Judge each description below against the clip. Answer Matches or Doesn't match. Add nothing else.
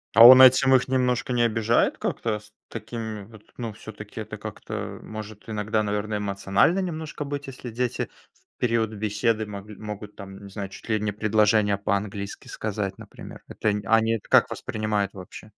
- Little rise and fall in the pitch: Matches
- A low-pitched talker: Matches